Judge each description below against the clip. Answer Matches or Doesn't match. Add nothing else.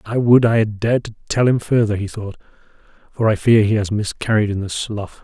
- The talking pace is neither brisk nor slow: Doesn't match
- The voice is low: Matches